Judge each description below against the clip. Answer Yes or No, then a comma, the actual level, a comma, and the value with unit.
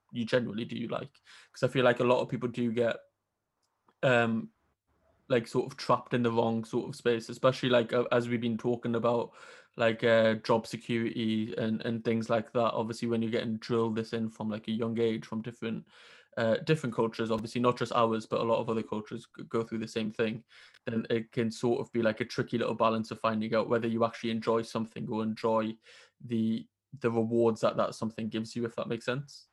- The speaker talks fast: Yes, fast, 220 wpm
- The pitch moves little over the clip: Yes, narrow, 1.1 semitones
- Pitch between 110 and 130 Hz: Yes, low, 115 Hz